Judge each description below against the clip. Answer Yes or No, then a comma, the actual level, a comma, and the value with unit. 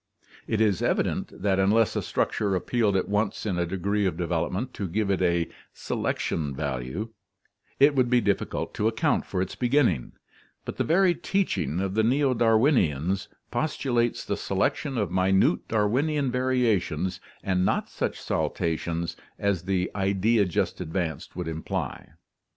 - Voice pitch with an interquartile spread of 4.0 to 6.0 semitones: Yes, average, 4.8 semitones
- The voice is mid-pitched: No, low, 100 Hz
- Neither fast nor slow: Yes, average, 150 wpm